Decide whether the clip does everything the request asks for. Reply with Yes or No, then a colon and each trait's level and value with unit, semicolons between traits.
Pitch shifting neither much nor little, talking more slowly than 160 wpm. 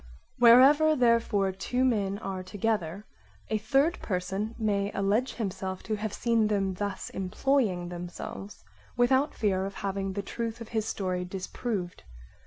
Yes: average, 3.5 semitones; average, 140 wpm